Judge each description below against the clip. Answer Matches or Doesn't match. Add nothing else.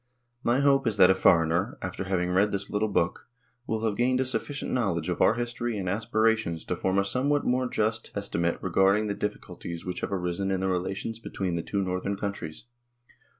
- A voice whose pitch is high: Doesn't match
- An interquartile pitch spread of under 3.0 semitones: Doesn't match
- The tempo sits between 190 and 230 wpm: Matches